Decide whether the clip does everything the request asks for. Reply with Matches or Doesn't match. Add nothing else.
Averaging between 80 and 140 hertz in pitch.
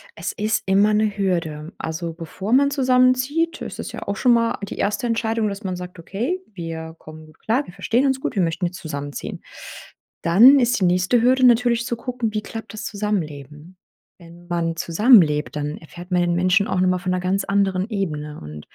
Doesn't match